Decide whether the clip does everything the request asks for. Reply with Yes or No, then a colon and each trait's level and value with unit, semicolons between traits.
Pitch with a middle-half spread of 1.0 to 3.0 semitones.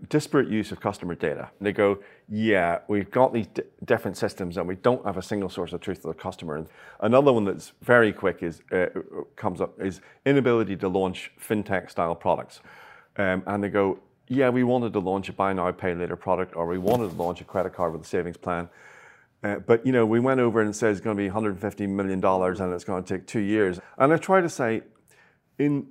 No: average, 3.6 semitones